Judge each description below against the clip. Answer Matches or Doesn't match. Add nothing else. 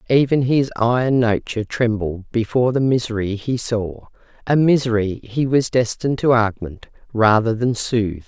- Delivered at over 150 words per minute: Doesn't match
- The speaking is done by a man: Doesn't match